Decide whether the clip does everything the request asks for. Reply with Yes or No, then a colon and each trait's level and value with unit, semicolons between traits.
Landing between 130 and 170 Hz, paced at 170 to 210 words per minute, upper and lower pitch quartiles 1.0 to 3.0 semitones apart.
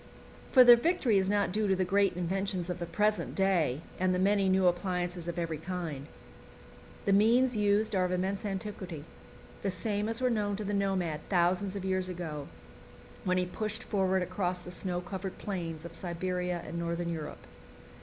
No: medium, 185 Hz; average, 185 wpm; narrow, 2.4 semitones